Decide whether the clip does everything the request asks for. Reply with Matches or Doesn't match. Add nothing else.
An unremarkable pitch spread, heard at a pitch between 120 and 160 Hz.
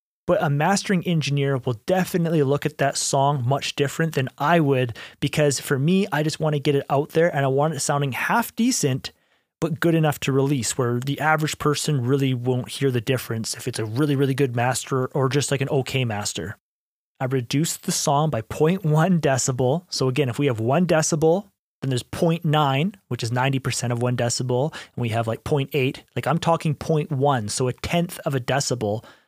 Matches